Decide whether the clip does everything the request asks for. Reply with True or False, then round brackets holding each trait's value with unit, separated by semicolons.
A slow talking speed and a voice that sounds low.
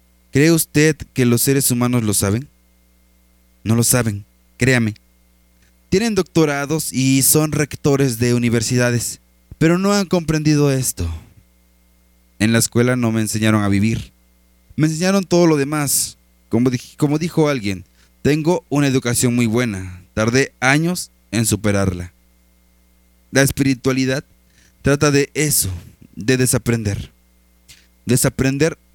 True (120 wpm; 120 Hz)